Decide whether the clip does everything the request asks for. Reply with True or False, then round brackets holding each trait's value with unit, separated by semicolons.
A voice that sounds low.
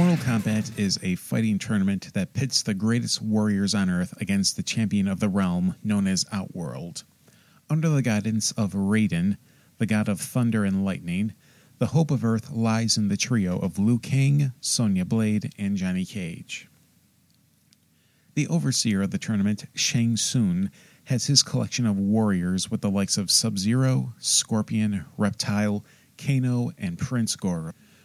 True (115 Hz)